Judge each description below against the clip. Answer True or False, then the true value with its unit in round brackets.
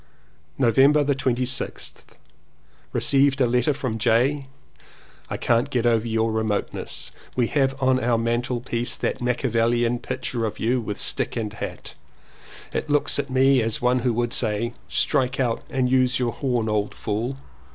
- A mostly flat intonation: True (2.3 semitones)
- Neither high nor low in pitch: False (125 Hz)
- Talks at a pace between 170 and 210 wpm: False (150 wpm)